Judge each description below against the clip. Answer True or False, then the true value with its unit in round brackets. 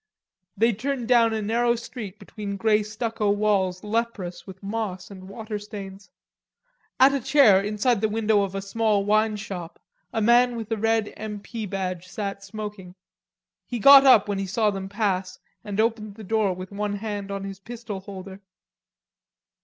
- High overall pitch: True (210 Hz)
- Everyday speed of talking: True (170 wpm)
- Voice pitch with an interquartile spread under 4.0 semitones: True (2.4 semitones)